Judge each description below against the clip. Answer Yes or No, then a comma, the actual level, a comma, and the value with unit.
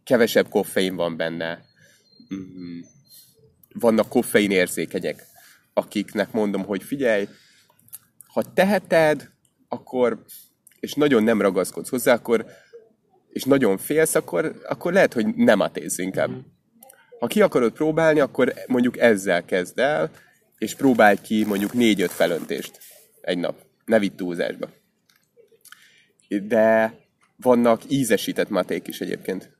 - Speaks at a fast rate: No, average, 120 wpm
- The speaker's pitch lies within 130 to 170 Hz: No, low, 110 Hz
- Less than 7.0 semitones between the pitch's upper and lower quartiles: No, wide, 8.0 semitones